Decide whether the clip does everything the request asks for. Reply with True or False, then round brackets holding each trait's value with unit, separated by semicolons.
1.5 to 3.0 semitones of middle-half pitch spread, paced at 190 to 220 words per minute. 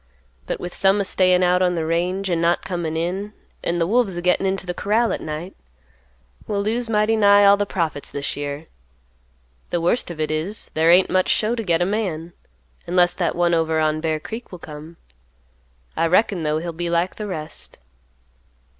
False (3.4 semitones; 200 wpm)